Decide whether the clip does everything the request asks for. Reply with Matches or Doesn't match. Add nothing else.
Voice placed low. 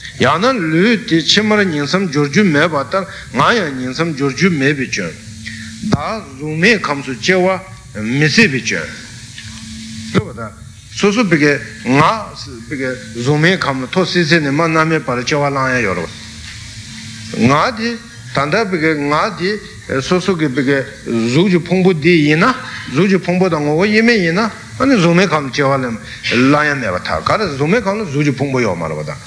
Doesn't match